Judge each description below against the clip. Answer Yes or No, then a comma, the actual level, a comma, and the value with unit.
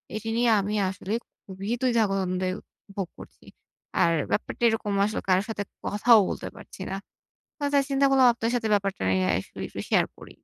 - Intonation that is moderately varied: Yes, average, 3.3 semitones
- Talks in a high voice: Yes, high, 205 Hz